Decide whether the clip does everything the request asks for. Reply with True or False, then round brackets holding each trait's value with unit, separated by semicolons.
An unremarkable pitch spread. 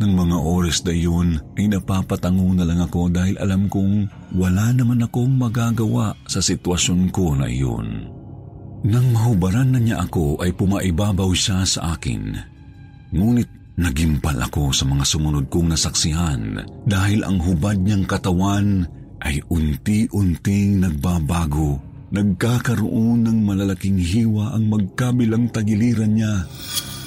True (4.4 semitones)